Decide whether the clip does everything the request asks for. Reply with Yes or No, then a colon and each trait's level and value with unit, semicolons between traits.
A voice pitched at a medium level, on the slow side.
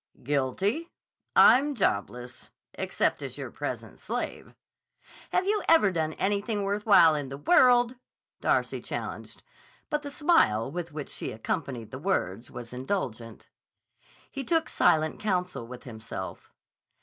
Yes: medium, 170 Hz; slow, 130 wpm